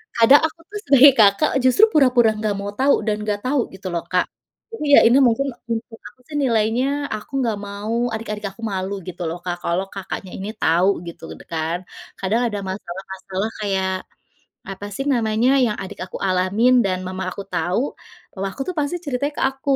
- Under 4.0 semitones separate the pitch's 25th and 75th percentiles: No, average, 4.7 semitones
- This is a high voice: Yes, high, 210 Hz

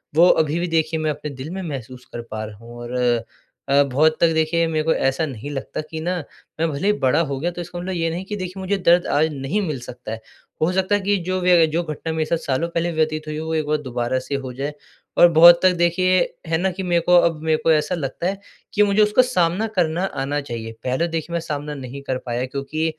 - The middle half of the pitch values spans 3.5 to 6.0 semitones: Yes, average, 4.1 semitones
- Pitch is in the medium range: Yes, medium, 160 Hz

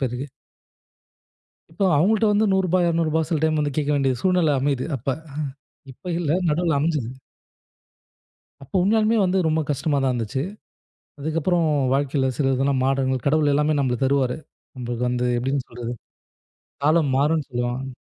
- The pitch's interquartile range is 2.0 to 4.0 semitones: Yes, average, 3.7 semitones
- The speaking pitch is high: No, medium, 145 Hz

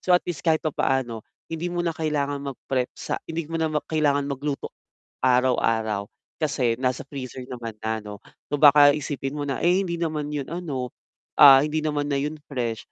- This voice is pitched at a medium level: Yes, medium, 145 Hz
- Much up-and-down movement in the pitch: No, average, 3.4 semitones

